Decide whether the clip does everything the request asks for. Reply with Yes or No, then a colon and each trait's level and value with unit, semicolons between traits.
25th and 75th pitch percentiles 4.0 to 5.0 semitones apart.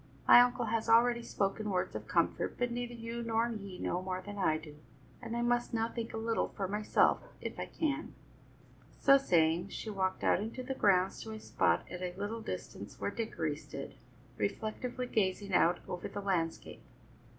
Yes: average, 4.4 semitones